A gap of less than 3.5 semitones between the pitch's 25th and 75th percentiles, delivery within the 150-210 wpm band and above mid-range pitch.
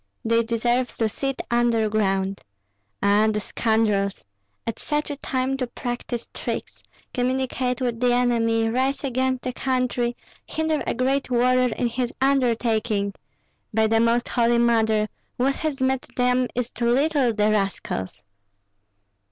No: narrow, 2.4 semitones; average, 140 wpm; high, 240 Hz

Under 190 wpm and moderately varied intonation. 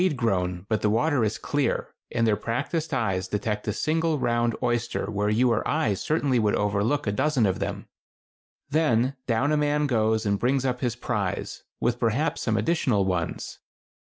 No: average, 200 wpm; average, 5.0 semitones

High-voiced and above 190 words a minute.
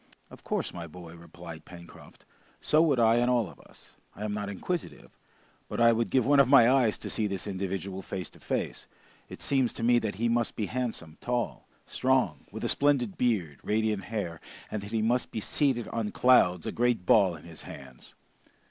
No: low, 110 Hz; average, 200 wpm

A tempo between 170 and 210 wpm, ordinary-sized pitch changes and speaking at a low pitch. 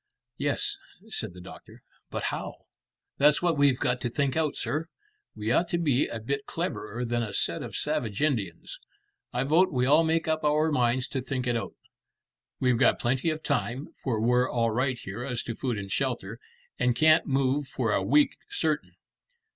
Yes: average, 185 wpm; average, 4.3 semitones; low, 130 Hz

